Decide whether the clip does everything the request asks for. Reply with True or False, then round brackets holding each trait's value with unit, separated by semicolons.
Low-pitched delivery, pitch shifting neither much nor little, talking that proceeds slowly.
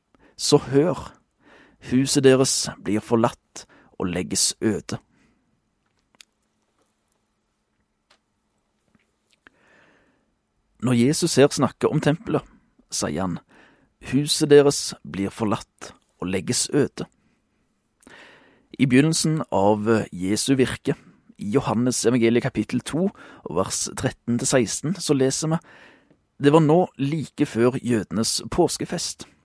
True (130 Hz; 4.1 semitones; 95 wpm)